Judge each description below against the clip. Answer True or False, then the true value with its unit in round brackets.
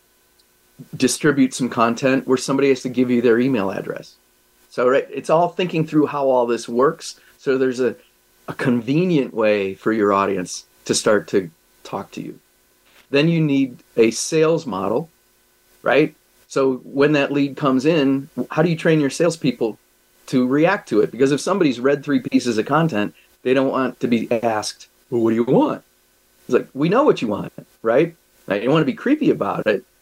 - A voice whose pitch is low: True (130 Hz)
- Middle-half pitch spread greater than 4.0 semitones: True (5.2 semitones)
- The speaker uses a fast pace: False (190 wpm)